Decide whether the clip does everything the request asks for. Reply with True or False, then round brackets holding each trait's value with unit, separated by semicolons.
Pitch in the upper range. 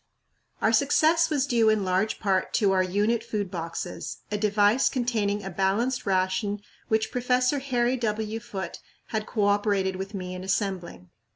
True (210 Hz)